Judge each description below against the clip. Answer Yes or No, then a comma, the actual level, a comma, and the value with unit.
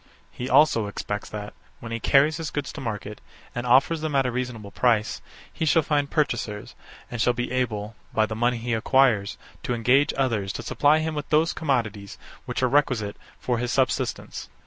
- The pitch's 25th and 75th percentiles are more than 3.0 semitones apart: Yes, average, 4.3 semitones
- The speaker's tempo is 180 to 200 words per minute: Yes, average, 190 wpm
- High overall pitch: No, low, 125 Hz